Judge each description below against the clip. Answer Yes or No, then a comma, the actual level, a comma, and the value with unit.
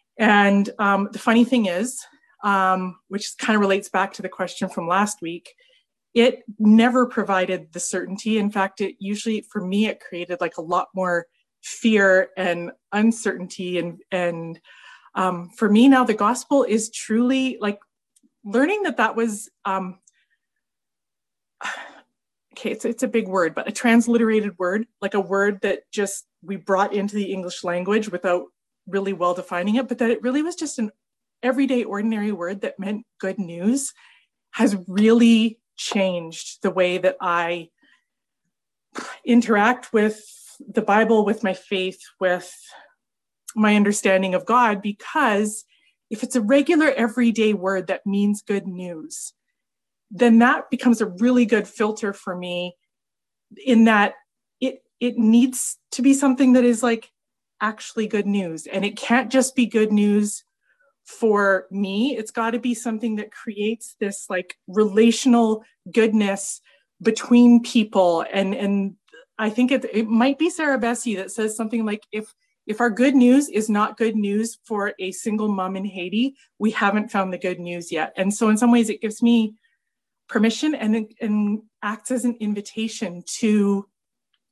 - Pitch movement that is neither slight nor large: Yes, average, 3.5 semitones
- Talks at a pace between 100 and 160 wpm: Yes, average, 155 wpm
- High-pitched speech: Yes, high, 215 Hz